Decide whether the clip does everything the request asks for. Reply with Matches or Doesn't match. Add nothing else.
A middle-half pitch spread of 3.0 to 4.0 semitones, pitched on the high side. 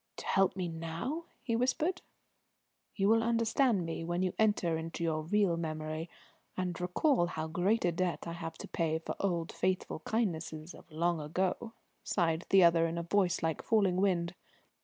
Doesn't match